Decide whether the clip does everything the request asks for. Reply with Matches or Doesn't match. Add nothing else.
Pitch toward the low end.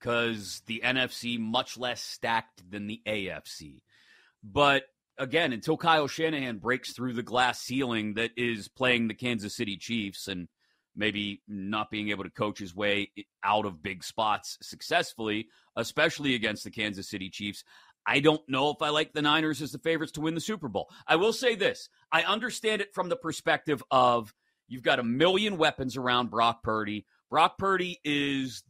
Matches